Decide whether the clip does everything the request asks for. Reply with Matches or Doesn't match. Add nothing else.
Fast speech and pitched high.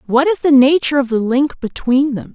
Matches